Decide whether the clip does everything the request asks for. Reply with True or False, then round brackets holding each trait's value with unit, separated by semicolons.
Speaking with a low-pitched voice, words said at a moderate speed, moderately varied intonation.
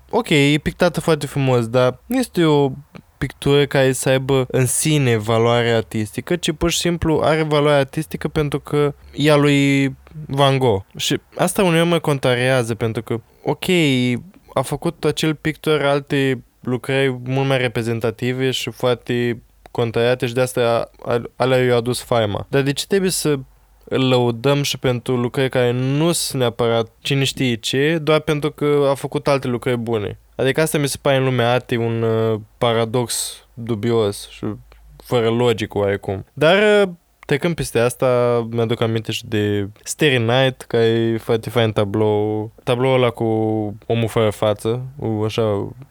True (130 Hz; 155 wpm; 3.8 semitones)